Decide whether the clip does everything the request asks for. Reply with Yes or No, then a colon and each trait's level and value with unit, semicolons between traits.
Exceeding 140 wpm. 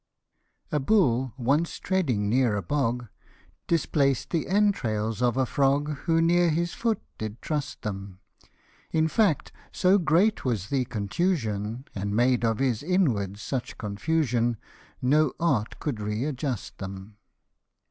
No: slow, 135 wpm